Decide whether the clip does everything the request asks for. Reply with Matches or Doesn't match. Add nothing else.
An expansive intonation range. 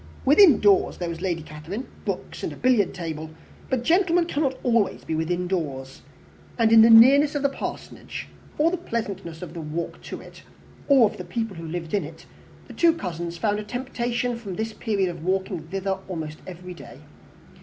Matches